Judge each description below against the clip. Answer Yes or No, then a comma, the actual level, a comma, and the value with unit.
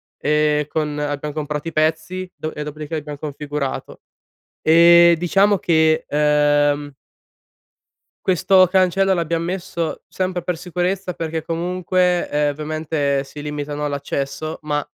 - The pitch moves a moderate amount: Yes, average, 3.0 semitones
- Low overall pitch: No, medium, 155 Hz